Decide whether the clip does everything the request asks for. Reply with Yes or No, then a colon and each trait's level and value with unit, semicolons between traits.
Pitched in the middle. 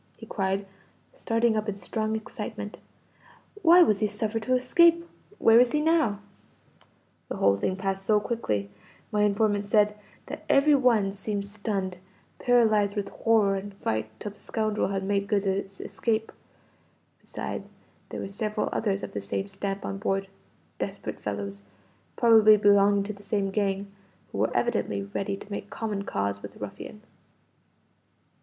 No: high, 205 Hz